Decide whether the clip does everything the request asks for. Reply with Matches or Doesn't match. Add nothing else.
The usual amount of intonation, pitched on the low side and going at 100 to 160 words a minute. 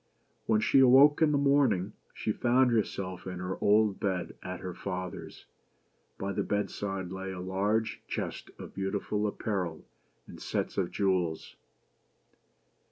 Matches